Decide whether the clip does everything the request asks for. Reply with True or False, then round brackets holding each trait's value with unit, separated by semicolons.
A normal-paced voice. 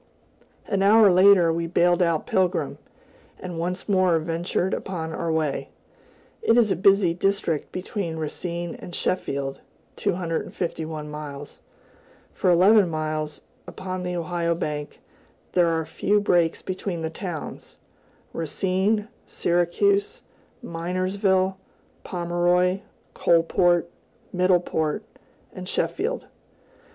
False (105 wpm)